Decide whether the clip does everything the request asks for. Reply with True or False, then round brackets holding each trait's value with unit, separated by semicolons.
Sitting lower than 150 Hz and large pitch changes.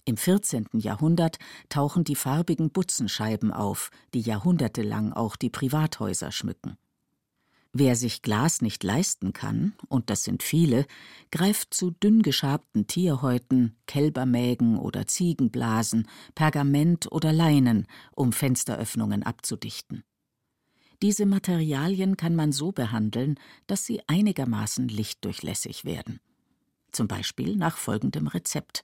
True (140 Hz; 6.7 semitones)